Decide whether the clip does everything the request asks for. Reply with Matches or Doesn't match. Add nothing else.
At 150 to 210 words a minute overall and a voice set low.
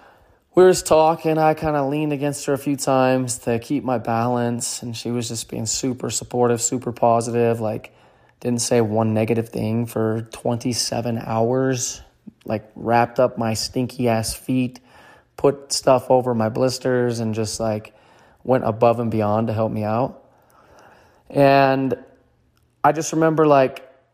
Matches